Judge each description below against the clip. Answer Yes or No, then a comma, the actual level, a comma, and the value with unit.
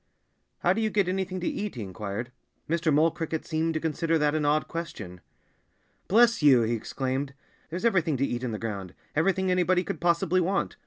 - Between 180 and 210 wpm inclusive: Yes, average, 195 wpm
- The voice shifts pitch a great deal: Yes, wide, 5.9 semitones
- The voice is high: No, medium, 160 Hz